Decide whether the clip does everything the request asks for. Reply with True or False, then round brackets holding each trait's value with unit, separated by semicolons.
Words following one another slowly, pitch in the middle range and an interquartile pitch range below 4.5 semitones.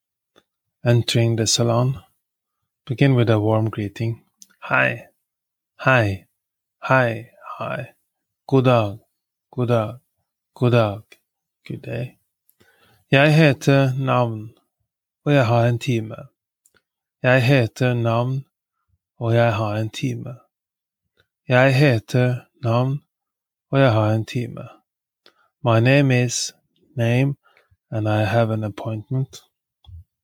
False (95 wpm; 120 Hz; 3.1 semitones)